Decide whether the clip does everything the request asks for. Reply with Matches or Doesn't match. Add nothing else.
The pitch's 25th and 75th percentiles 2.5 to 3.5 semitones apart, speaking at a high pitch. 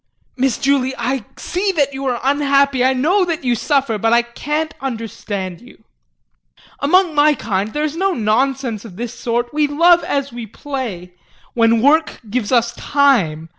Doesn't match